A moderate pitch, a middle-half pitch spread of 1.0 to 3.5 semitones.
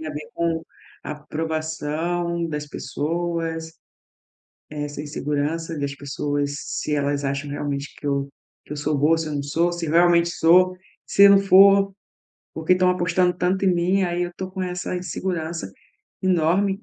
Yes: medium, 165 Hz; average, 3.2 semitones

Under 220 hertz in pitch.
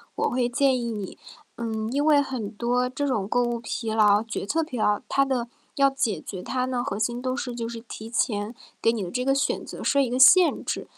No: high, 240 Hz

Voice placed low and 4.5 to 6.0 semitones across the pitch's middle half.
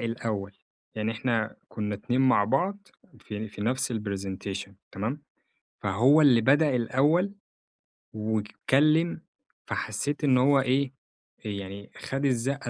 Yes: low, 120 Hz; average, 4.9 semitones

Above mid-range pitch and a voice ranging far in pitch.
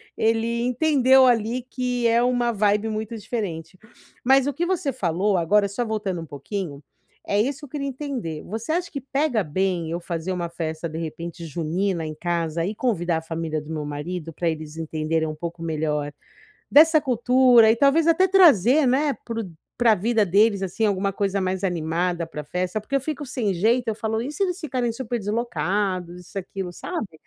Yes: high, 205 Hz; wide, 6.6 semitones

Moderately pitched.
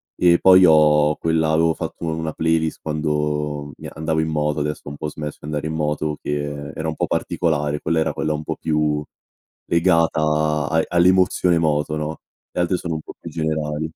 No: very low, 80 Hz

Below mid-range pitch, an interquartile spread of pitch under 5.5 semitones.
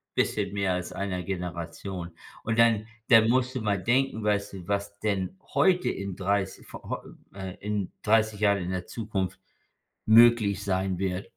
Yes: low, 100 Hz; narrow, 2.6 semitones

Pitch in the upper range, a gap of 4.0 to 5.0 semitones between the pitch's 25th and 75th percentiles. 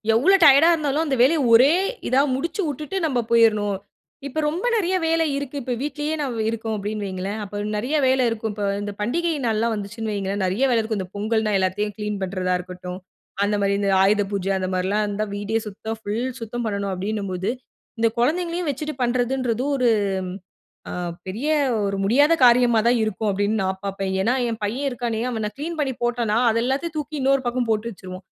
Yes: high, 225 Hz; average, 4.7 semitones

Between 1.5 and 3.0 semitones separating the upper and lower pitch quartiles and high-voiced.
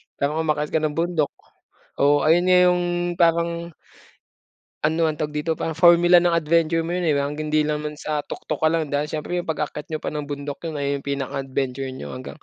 No: narrow, 2.5 semitones; medium, 155 Hz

